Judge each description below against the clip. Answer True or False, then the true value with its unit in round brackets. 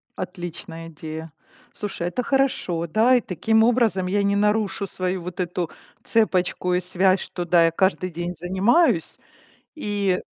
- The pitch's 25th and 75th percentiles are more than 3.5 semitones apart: False (3.1 semitones)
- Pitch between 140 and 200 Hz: True (185 Hz)